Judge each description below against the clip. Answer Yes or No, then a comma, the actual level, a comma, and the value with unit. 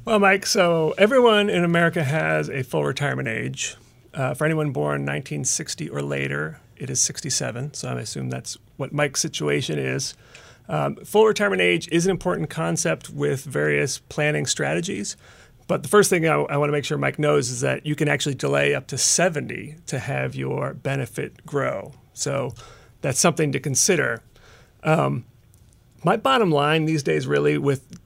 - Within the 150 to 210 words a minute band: Yes, average, 170 wpm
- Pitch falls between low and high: Yes, medium, 145 Hz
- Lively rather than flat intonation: Yes, wide, 8.7 semitones